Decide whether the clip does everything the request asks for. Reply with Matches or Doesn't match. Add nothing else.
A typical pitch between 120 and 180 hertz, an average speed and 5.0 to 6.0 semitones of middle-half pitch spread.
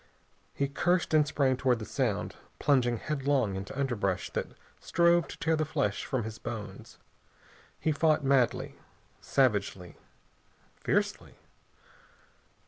Doesn't match